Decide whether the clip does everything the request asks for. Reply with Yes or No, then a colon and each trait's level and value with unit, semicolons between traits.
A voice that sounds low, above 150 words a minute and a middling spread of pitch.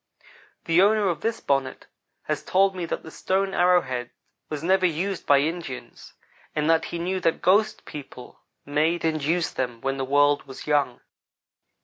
No: medium, 160 Hz; average, 170 wpm; average, 4.6 semitones